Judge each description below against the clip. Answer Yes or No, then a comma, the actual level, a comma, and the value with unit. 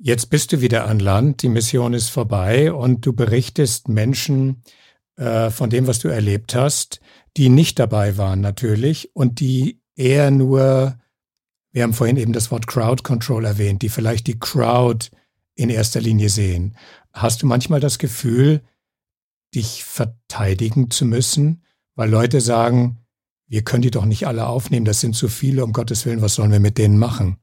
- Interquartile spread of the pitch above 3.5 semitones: No, average, 2.9 semitones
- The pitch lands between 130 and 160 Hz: No, low, 120 Hz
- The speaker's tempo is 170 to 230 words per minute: Yes, average, 175 wpm